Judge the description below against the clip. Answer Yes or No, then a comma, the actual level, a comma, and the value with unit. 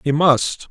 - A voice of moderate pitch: Yes, medium, 150 Hz